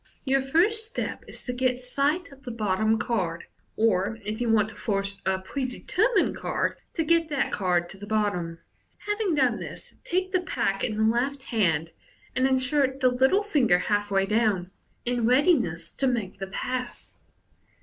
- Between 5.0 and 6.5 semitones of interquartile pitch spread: Yes, wide, 5.6 semitones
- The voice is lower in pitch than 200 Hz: No, high, 240 Hz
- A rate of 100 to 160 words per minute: No, average, 175 wpm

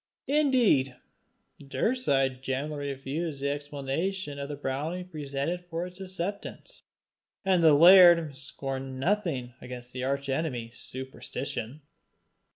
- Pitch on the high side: No, medium, 145 Hz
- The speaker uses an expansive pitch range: No, average, 4.7 semitones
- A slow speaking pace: Yes, slow, 110 wpm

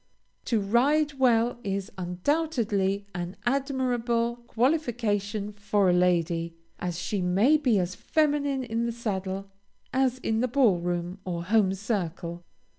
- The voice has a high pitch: Yes, high, 210 Hz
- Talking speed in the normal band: No, slow, 130 wpm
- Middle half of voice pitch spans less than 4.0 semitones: No, average, 5.1 semitones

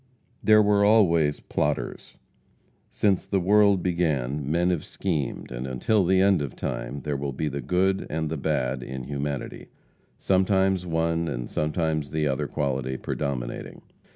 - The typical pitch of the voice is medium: No, very low, 80 Hz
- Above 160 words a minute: No, average, 150 wpm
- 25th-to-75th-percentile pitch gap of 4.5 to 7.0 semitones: Yes, average, 5.2 semitones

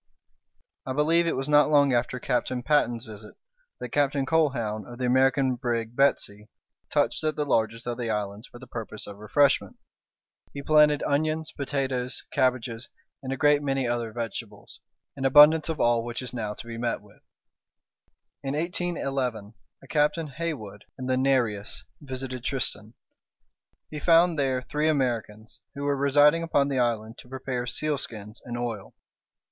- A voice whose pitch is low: Yes, low, 130 Hz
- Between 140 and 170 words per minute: Yes, average, 160 wpm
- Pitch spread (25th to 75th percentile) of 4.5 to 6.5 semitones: No, average, 3.7 semitones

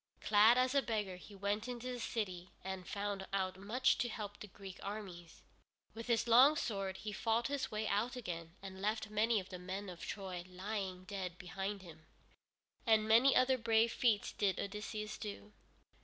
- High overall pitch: Yes, high, 205 Hz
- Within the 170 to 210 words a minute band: Yes, average, 180 wpm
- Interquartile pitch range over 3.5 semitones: No, average, 3.1 semitones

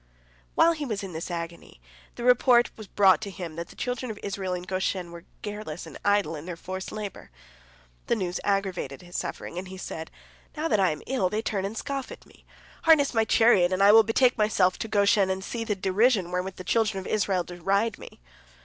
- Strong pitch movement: No, average, 3.5 semitones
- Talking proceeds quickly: Yes, fast, 215 wpm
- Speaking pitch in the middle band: No, high, 195 Hz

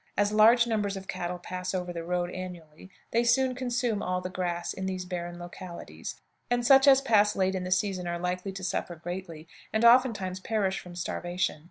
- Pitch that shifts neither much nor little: Yes, average, 3.5 semitones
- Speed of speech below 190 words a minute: No, average, 195 wpm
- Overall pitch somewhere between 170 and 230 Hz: Yes, medium, 185 Hz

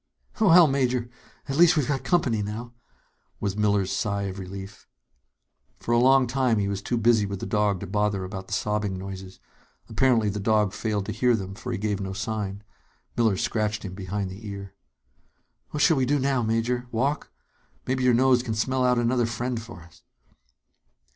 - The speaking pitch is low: Yes, low, 110 Hz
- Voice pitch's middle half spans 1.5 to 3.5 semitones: No, average, 3.9 semitones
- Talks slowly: No, average, 185 wpm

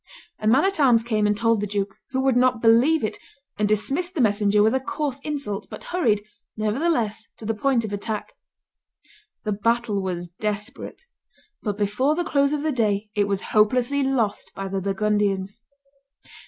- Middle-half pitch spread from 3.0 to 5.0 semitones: Yes, average, 4.2 semitones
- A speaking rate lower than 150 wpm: No, average, 175 wpm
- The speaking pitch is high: Yes, high, 220 Hz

